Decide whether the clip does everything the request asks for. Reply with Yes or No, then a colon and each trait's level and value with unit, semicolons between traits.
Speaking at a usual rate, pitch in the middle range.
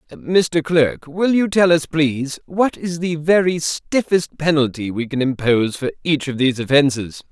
Yes: average, 170 wpm; medium, 155 Hz